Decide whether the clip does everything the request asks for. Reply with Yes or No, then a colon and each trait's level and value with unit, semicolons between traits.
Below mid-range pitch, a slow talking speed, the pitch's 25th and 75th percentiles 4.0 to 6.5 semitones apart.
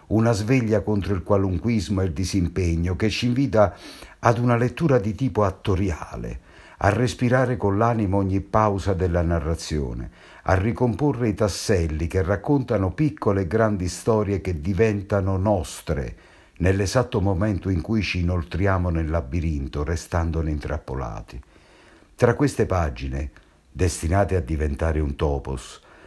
No: very low, 95 Hz; average, 130 wpm; average, 4.5 semitones